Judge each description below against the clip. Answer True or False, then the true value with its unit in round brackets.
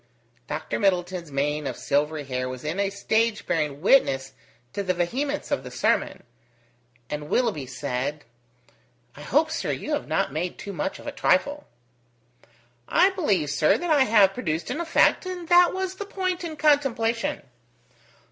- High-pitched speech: True (195 Hz)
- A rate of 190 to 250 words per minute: False (160 wpm)